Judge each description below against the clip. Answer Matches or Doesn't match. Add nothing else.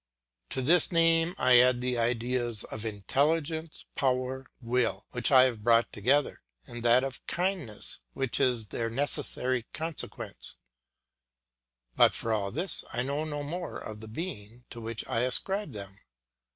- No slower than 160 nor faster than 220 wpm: Doesn't match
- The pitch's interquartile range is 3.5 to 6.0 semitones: Matches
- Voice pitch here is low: Matches